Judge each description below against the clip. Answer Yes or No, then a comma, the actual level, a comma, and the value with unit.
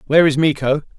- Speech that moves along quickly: No, average, 185 wpm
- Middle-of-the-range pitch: Yes, medium, 150 Hz